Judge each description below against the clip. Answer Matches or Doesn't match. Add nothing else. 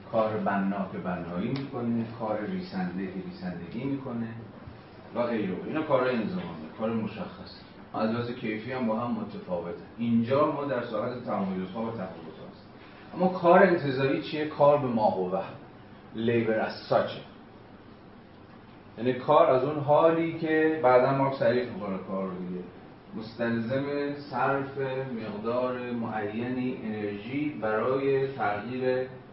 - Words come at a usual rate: Matches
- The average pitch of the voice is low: Matches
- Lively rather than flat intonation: Doesn't match